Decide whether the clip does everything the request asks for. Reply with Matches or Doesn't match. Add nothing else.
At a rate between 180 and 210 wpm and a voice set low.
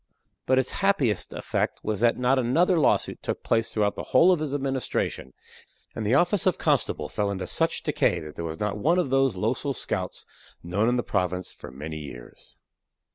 Matches